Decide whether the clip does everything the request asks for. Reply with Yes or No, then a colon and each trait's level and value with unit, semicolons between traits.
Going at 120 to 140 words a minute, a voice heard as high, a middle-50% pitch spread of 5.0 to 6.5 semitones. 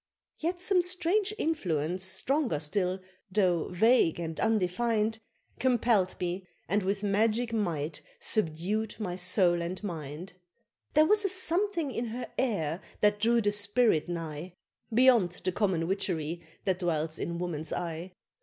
Yes: slow, 135 wpm; high, 195 Hz; wide, 5.4 semitones